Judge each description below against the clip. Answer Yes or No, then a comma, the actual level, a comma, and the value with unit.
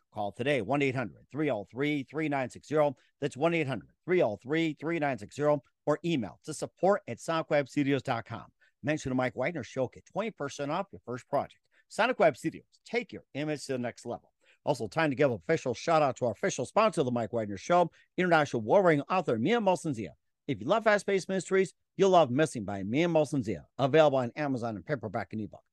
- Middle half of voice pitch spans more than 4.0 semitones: Yes, average, 4.9 semitones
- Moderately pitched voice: Yes, medium, 145 Hz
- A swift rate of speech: No, average, 185 wpm